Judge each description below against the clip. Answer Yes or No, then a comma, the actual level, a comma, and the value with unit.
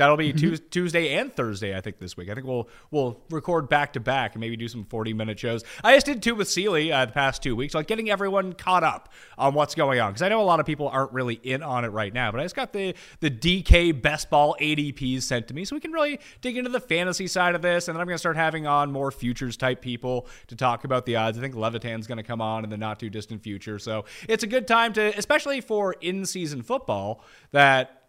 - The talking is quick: Yes, fast, 265 wpm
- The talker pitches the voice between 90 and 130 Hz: No, medium, 140 Hz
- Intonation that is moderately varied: No, wide, 6.7 semitones